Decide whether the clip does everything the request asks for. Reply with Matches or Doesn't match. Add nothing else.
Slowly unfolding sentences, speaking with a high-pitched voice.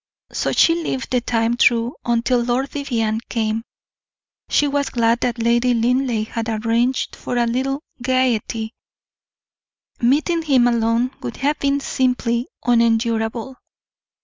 Matches